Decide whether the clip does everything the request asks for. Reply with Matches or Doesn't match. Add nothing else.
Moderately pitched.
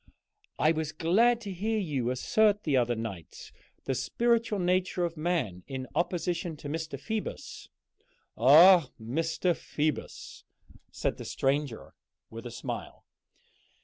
Matches